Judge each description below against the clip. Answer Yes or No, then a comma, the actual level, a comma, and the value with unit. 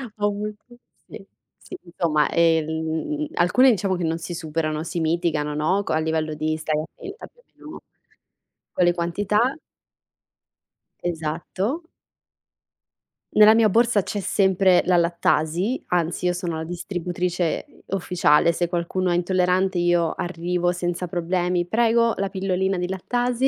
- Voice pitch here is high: No, medium, 175 Hz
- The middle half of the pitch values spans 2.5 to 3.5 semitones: Yes, average, 2.8 semitones